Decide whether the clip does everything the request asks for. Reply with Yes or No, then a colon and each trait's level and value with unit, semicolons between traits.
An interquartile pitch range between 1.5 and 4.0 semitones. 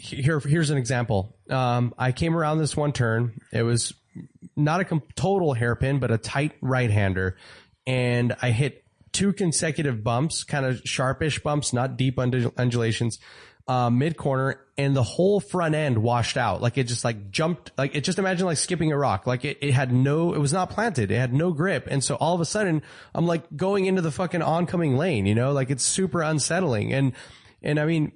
No: average, 4.7 semitones